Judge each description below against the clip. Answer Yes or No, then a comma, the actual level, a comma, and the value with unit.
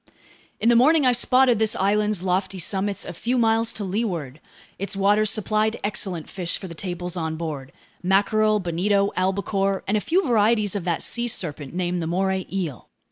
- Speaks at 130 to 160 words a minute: No, average, 180 wpm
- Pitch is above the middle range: Yes, high, 195 Hz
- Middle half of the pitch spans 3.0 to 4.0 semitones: Yes, average, 3.3 semitones